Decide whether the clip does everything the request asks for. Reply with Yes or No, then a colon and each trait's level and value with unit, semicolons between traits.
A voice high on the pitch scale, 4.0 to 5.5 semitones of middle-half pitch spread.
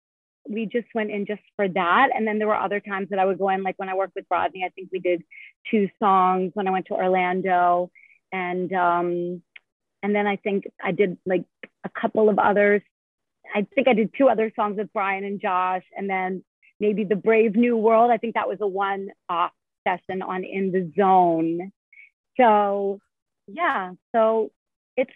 No: high, 195 Hz; narrow, 2.5 semitones